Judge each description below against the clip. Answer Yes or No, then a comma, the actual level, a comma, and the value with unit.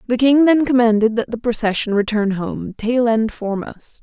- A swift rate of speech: No, average, 180 wpm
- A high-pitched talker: Yes, high, 230 Hz